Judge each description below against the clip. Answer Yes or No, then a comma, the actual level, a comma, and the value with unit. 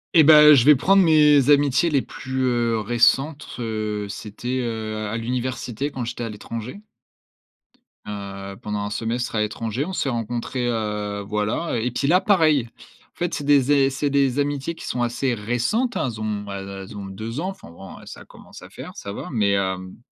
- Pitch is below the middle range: Yes, low, 120 Hz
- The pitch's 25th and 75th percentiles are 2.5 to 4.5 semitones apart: No, average, 5.1 semitones